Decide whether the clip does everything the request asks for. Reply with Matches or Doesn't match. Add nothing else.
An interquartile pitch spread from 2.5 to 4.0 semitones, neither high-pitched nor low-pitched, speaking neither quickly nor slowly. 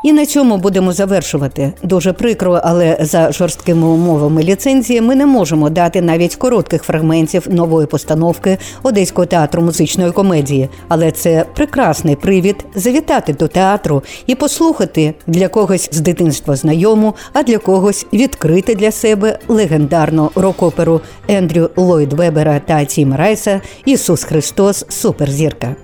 Doesn't match